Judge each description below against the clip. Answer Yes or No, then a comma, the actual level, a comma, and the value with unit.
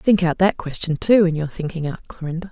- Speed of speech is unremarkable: No, fast, 240 wpm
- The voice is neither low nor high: Yes, medium, 170 Hz